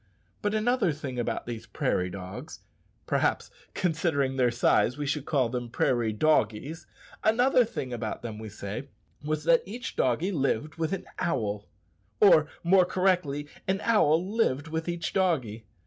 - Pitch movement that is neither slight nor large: No, wide, 7.1 semitones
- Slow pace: No, average, 150 wpm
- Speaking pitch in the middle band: Yes, medium, 150 Hz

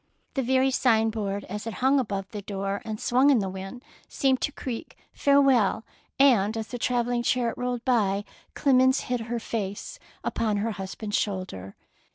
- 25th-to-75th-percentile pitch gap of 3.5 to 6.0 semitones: Yes, average, 4.0 semitones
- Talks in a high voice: Yes, high, 230 Hz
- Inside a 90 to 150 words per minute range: No, average, 170 wpm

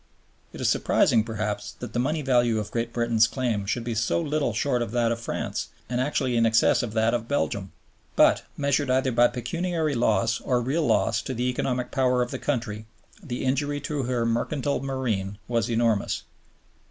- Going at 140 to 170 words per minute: No, average, 190 wpm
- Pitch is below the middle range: Yes, low, 120 Hz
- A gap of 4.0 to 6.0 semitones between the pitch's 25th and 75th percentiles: No, narrow, 2.6 semitones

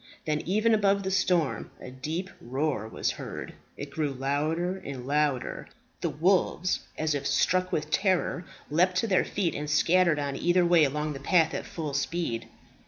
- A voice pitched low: No, medium, 160 Hz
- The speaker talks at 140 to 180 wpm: Yes, average, 170 wpm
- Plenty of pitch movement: No, average, 4.3 semitones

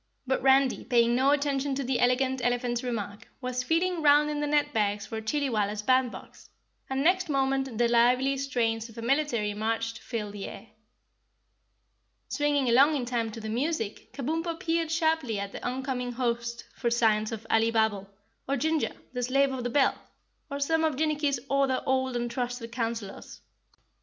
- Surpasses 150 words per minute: Yes, average, 170 wpm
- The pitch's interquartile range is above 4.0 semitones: No, average, 3.4 semitones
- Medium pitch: No, very high, 255 Hz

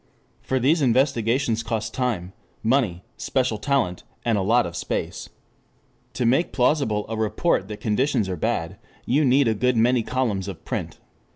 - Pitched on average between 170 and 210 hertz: No, low, 115 Hz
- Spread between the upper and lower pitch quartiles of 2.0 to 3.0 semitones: No, average, 3.8 semitones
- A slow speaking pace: No, average, 160 wpm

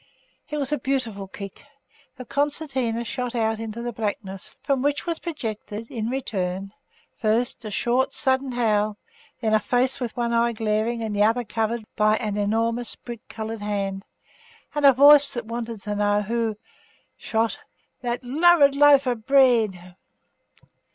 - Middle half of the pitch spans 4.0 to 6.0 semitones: No, average, 3.3 semitones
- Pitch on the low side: No, high, 230 Hz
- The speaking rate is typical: Yes, average, 155 wpm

